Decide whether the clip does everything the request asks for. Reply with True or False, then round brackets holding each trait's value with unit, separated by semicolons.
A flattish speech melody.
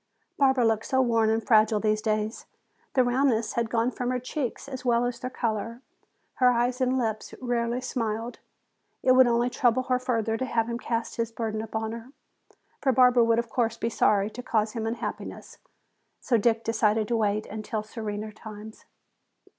True (2.2 semitones)